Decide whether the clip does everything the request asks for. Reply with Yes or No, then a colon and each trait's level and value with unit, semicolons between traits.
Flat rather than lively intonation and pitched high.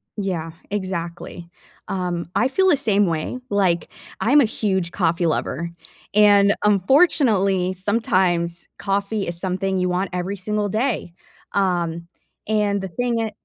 No: average, 3.2 semitones; high, 195 Hz